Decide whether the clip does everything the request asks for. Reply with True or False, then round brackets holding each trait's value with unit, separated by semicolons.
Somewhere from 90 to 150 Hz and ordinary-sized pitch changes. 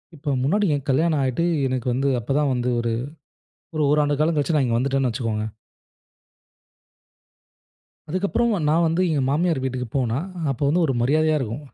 True (140 Hz; 3.5 semitones)